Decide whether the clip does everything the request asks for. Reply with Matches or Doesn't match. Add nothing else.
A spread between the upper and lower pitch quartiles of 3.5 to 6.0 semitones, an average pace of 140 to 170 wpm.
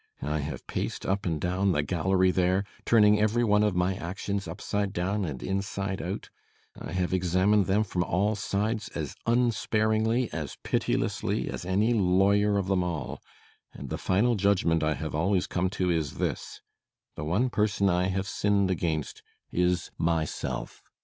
Doesn't match